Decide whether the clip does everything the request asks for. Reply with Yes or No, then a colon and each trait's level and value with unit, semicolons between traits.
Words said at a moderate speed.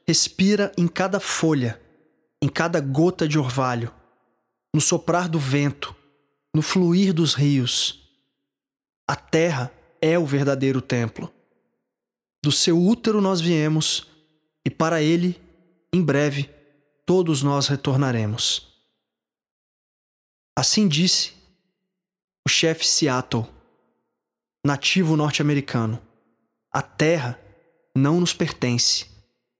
No: slow, 95 wpm